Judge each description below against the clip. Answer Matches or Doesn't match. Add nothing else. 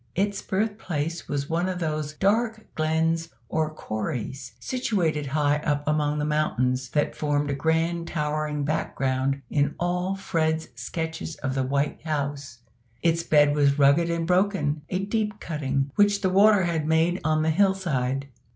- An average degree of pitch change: Matches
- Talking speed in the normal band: Matches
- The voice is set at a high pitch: Doesn't match